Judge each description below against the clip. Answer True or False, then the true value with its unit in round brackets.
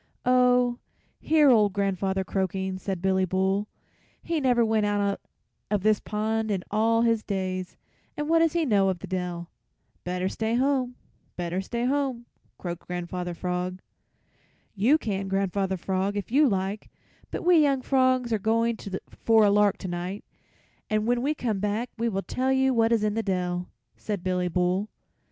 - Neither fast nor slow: True (165 wpm)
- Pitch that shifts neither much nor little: True (4.2 semitones)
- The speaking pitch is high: True (205 Hz)